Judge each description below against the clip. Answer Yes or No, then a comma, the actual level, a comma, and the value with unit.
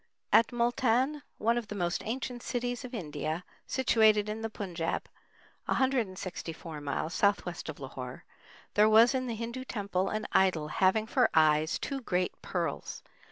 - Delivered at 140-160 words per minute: Yes, average, 150 wpm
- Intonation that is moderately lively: No, wide, 5.8 semitones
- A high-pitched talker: Yes, high, 210 Hz